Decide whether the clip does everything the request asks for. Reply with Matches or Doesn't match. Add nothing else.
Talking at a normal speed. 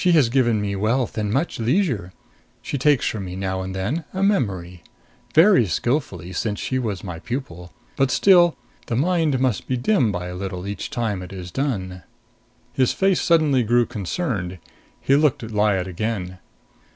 Matches